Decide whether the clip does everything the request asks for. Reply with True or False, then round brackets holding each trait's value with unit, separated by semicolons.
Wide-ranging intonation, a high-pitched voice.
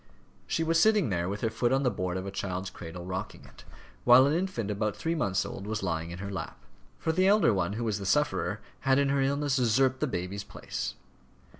False (6.6 semitones; 110 Hz)